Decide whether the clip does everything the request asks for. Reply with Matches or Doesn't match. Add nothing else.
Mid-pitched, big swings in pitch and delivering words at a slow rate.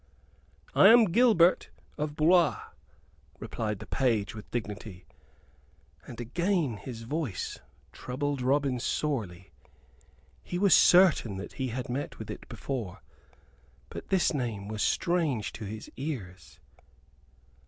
Doesn't match